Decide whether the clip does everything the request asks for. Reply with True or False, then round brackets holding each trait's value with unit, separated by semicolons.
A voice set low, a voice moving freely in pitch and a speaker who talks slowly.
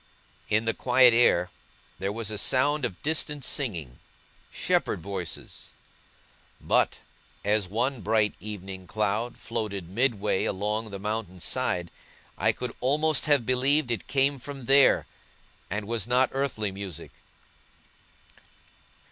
False (110 Hz; 4.5 semitones; 120 wpm)